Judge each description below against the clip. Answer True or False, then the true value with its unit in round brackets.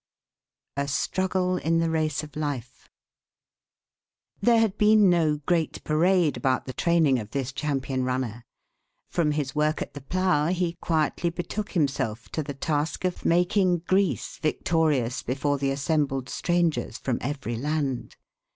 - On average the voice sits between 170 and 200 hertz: False (155 Hz)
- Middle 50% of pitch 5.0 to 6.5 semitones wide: False (4.3 semitones)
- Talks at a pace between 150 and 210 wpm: False (140 wpm)